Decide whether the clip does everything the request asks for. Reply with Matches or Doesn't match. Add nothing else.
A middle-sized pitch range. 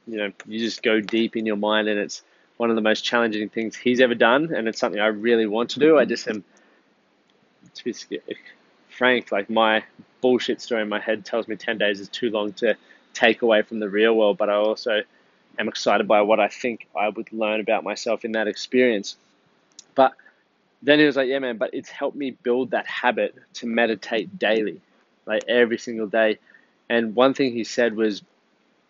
Doesn't match